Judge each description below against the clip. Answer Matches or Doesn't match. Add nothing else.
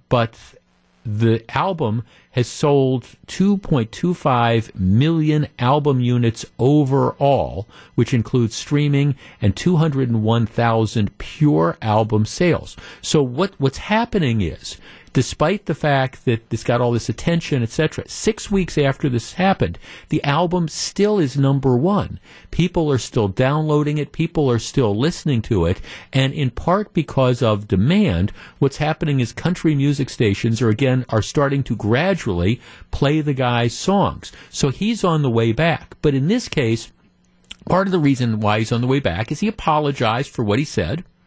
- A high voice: Doesn't match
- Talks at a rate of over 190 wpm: Doesn't match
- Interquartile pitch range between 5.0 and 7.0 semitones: Matches